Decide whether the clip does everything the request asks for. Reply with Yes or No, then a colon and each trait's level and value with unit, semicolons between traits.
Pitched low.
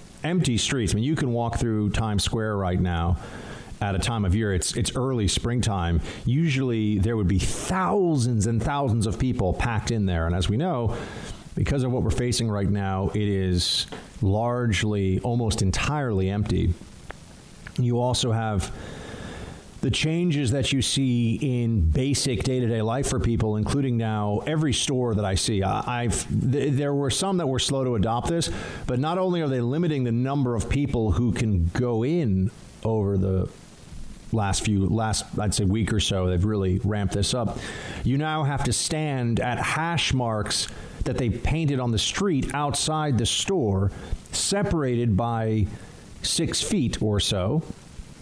Yes: low, 115 Hz